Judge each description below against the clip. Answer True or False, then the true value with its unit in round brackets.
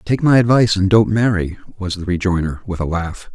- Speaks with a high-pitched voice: False (100 Hz)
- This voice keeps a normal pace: False (215 wpm)